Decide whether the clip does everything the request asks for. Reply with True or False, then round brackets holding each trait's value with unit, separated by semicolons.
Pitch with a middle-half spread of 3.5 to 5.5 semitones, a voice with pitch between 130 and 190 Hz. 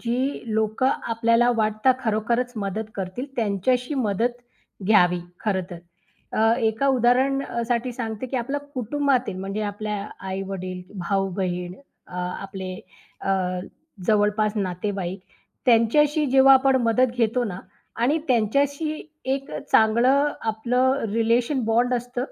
False (3.9 semitones; 230 Hz)